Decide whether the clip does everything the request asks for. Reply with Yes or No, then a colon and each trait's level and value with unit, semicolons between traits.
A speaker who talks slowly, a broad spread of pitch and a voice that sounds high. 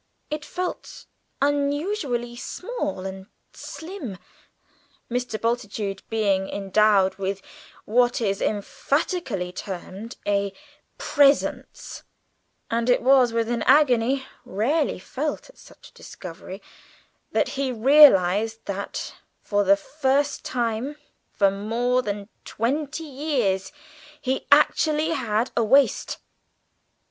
Yes: slow, 105 wpm; wide, 5.8 semitones; high, 235 Hz